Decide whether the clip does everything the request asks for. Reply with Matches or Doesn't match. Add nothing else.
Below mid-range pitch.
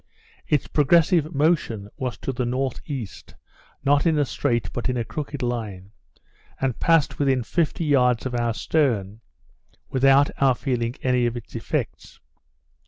Matches